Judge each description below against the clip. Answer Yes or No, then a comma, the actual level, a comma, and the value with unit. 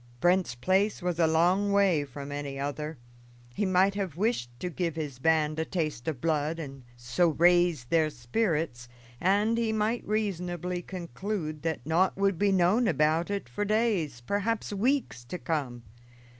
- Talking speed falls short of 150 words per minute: No, average, 160 wpm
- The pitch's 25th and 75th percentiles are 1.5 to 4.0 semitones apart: No, average, 4.8 semitones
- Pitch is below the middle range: No, medium, 170 Hz